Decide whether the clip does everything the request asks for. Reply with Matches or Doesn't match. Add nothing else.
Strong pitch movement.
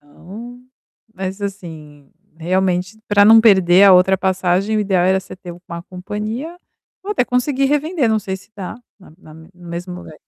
Doesn't match